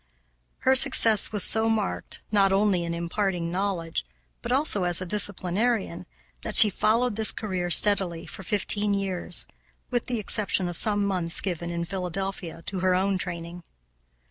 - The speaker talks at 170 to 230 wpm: No, average, 155 wpm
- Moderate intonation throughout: Yes, average, 3.1 semitones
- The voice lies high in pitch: Yes, high, 195 Hz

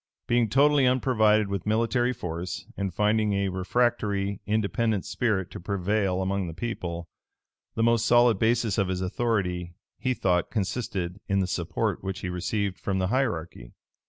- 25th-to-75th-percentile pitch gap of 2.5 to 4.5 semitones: Yes, average, 3.9 semitones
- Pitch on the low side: Yes, low, 100 Hz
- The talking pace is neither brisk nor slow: Yes, average, 155 wpm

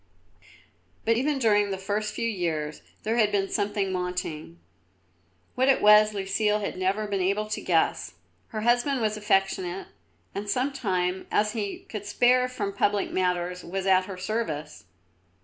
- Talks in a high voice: Yes, high, 205 Hz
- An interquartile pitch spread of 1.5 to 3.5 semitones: Yes, narrow, 2.6 semitones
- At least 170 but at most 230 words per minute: No, average, 155 wpm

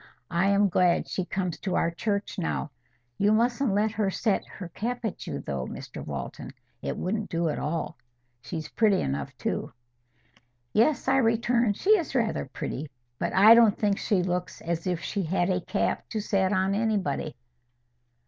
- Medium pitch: No, high, 195 Hz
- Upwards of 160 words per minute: Yes, average, 175 wpm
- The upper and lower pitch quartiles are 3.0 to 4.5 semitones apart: Yes, average, 4.2 semitones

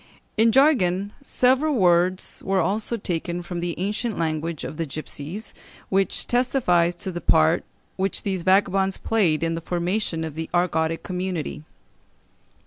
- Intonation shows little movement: No, average, 3.4 semitones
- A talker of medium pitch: Yes, medium, 180 Hz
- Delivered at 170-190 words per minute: No, average, 140 wpm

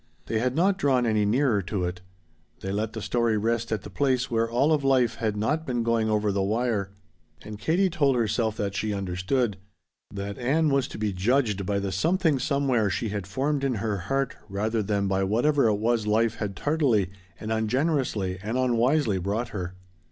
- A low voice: Yes, low, 110 Hz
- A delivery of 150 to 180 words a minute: No, average, 195 wpm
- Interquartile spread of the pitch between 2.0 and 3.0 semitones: No, average, 4.3 semitones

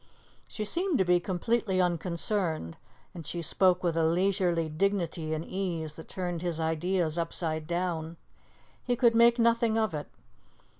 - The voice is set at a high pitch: No, medium, 175 Hz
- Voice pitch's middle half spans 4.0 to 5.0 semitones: No, average, 3.4 semitones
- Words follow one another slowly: No, average, 150 wpm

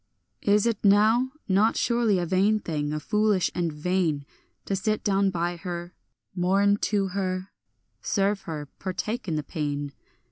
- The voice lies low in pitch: No, high, 190 Hz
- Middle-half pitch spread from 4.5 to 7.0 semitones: No, average, 3.2 semitones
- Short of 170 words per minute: Yes, average, 150 wpm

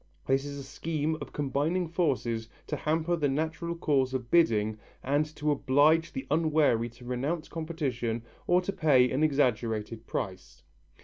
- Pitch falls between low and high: Yes, medium, 145 Hz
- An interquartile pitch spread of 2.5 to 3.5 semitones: No, average, 4.4 semitones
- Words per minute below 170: Yes, average, 150 wpm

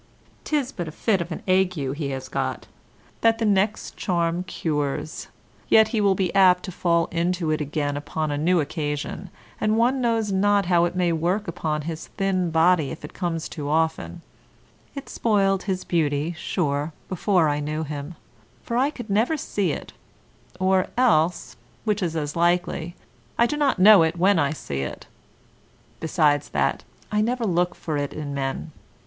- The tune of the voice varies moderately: Yes, average, 4.3 semitones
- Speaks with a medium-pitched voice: Yes, medium, 175 Hz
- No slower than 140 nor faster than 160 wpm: No, average, 175 wpm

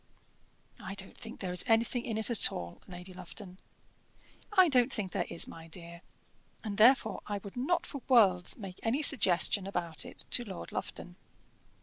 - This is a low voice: No, high, 200 Hz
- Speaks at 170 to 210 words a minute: Yes, average, 175 wpm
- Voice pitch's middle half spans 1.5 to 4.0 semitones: No, average, 5.0 semitones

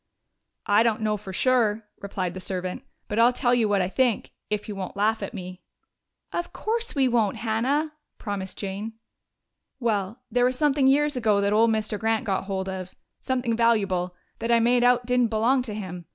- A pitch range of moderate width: Yes, average, 3.8 semitones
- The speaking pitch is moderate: No, high, 220 Hz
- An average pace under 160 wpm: No, average, 190 wpm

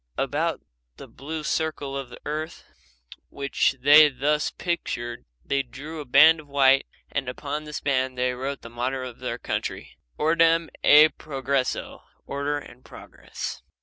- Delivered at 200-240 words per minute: No, average, 150 wpm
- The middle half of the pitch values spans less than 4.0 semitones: Yes, narrow, 2.6 semitones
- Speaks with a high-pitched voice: No, medium, 140 Hz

